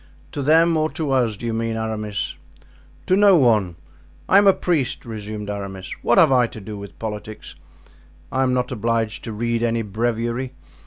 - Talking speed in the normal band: Yes, average, 180 wpm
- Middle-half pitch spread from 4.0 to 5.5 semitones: No, average, 3.5 semitones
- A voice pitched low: Yes, low, 115 Hz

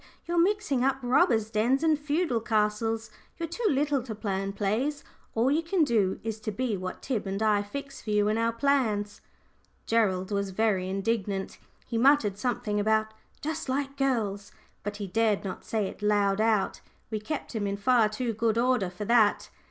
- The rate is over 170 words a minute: Yes, average, 185 wpm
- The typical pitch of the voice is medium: No, high, 220 Hz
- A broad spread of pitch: No, average, 4.3 semitones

